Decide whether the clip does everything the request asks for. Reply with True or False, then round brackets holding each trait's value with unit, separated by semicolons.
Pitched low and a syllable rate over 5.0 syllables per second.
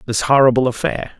True (125 Hz; 6.1 syllables/s)